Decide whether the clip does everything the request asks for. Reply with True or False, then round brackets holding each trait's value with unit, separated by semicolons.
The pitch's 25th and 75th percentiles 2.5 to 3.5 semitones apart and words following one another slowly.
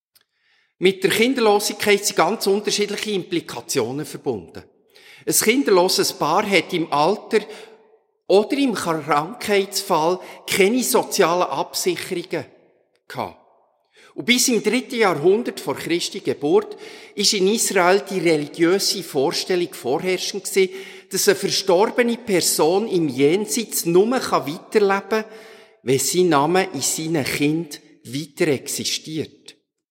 False (4.0 semitones; 110 wpm)